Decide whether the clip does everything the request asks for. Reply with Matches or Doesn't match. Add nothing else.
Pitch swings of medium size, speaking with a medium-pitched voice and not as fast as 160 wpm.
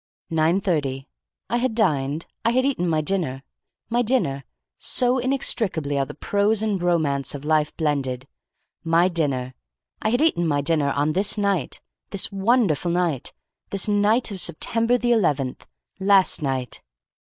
Doesn't match